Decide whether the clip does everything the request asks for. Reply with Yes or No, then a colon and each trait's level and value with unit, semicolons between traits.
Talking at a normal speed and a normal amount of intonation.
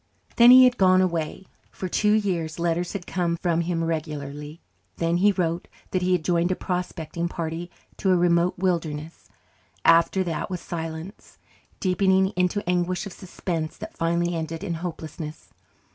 No: average, 160 wpm; narrow, 2.1 semitones